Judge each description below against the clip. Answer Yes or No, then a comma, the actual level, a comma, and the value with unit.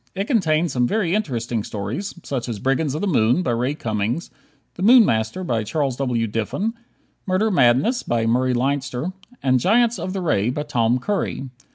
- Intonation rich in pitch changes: Yes, wide, 7.8 semitones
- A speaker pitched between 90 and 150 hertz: Yes, low, 135 Hz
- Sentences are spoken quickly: No, average, 180 wpm